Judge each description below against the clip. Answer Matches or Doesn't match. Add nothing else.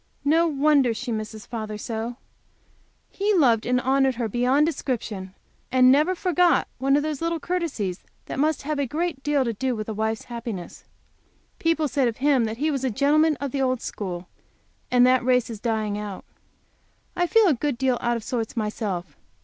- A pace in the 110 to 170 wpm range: Doesn't match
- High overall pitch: Matches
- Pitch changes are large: Doesn't match